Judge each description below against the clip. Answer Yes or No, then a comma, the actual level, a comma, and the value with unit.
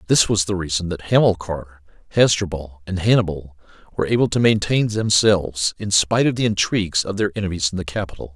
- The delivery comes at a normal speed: Yes, average, 180 wpm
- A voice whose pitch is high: No, very low, 95 Hz